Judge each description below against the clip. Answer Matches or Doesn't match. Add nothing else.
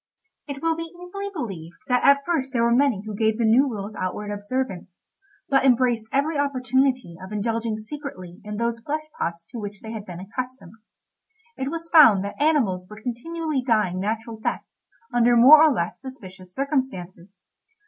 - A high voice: Matches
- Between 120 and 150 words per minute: Doesn't match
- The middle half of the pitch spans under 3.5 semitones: Doesn't match